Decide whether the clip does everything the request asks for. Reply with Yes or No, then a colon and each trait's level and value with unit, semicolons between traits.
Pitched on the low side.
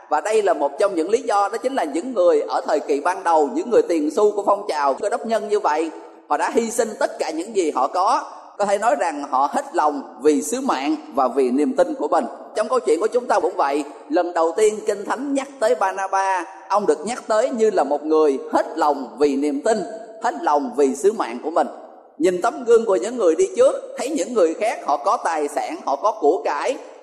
No: high, 220 Hz